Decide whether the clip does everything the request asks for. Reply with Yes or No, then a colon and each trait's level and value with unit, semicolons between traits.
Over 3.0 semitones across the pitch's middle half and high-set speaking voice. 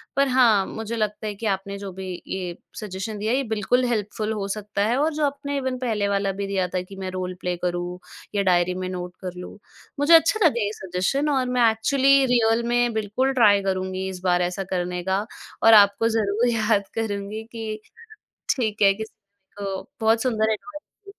Yes: average, 3.8 semitones; high, 210 Hz